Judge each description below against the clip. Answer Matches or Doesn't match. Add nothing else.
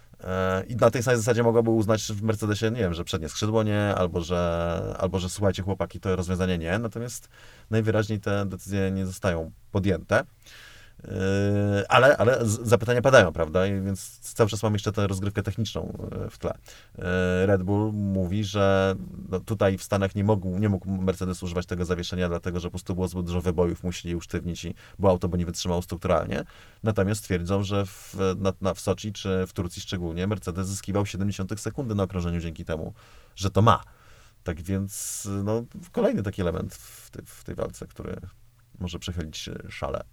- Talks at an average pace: Doesn't match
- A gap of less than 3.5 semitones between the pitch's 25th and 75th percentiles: Matches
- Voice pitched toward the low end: Matches